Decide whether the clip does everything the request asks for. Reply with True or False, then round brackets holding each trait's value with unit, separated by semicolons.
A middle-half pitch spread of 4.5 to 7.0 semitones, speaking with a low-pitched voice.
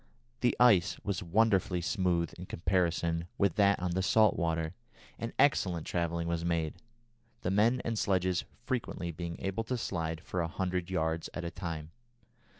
False (3.0 semitones; 90 Hz)